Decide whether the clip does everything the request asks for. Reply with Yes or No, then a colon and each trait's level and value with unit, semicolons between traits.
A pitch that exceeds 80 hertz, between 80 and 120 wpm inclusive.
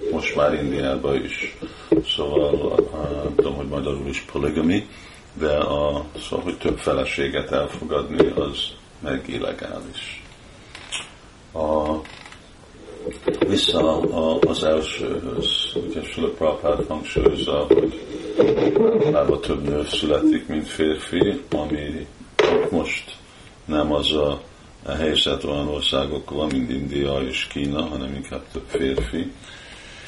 No: very low, 75 Hz; average, 110 wpm